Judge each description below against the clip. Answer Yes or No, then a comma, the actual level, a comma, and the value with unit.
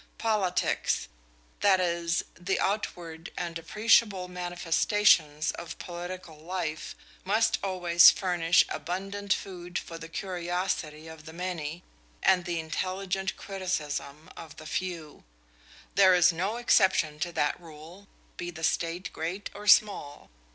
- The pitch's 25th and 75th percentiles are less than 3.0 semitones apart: Yes, narrow, 2.6 semitones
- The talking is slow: Yes, slow, 125 wpm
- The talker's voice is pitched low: No, medium, 175 Hz